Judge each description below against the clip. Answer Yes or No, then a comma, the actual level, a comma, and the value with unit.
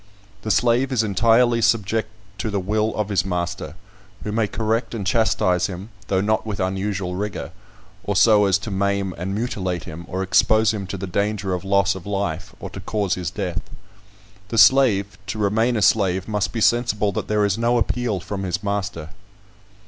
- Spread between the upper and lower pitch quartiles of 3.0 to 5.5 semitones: No, narrow, 2.6 semitones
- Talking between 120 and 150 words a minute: No, average, 185 wpm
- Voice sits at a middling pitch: No, low, 100 Hz